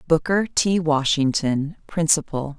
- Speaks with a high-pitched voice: No, medium, 155 Hz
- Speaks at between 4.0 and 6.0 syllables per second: No, 3.8 syllables/s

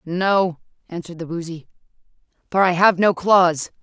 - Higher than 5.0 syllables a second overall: No, 4.7 syllables/s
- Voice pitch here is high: No, medium, 175 Hz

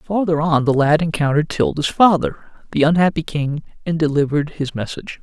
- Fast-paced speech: No, average, 160 wpm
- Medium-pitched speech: Yes, medium, 150 Hz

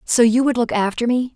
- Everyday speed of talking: No, fast, 265 wpm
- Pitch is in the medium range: No, high, 235 Hz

